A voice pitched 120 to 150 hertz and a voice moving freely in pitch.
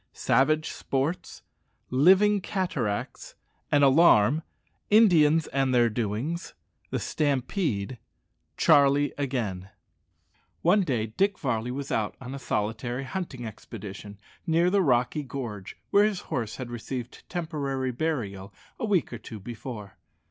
Yes: low, 135 Hz; wide, 5.9 semitones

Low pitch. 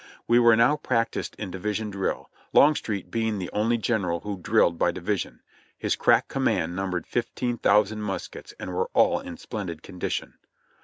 Yes: low, 105 Hz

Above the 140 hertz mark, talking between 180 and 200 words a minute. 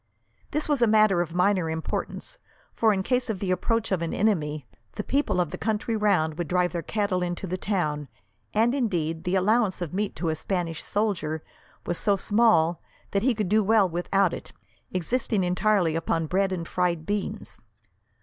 Yes: high, 190 Hz; average, 185 wpm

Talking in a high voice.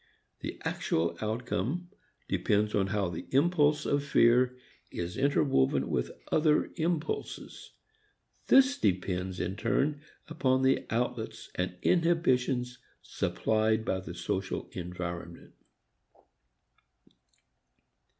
No: low, 120 Hz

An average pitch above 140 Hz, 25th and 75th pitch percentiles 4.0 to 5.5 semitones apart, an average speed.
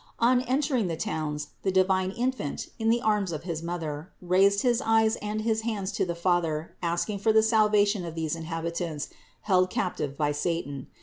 Yes: medium, 185 Hz; average, 4.9 semitones; average, 180 wpm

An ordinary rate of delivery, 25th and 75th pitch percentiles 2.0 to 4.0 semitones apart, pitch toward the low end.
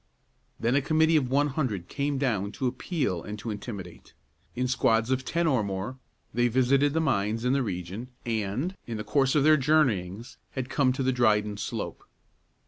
No: average, 185 wpm; average, 4.7 semitones; low, 125 Hz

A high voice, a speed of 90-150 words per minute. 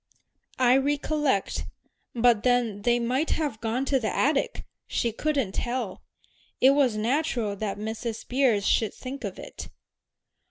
Yes: high, 245 Hz; slow, 135 wpm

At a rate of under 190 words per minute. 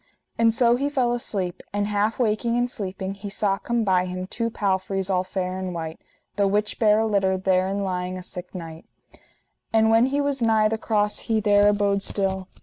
No: average, 200 wpm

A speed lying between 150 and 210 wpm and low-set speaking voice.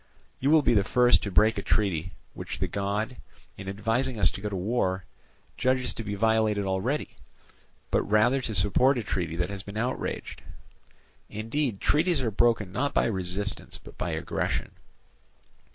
Yes: average, 170 wpm; low, 105 Hz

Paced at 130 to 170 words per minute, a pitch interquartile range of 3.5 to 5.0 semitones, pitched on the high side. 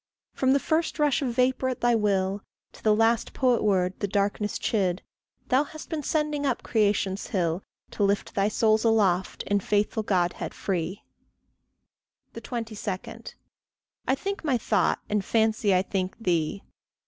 Yes: average, 150 wpm; average, 4.4 semitones; high, 215 Hz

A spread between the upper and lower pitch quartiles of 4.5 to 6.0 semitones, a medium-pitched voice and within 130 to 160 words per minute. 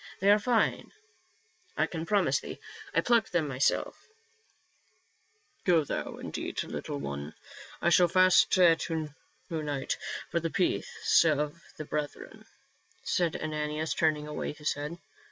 No: average, 3.2 semitones; medium, 160 Hz; slow, 135 wpm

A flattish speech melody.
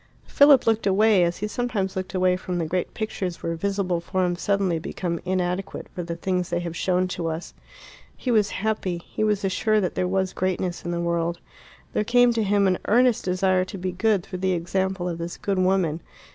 Yes: narrow, 2.3 semitones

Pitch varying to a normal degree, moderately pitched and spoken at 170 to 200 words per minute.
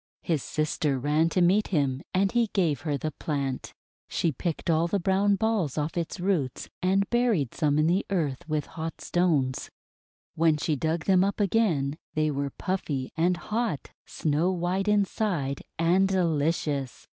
No: average, 4.4 semitones; medium, 165 Hz; average, 160 wpm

